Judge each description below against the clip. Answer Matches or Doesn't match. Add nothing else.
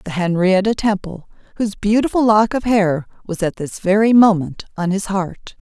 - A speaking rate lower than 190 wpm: Matches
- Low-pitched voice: Doesn't match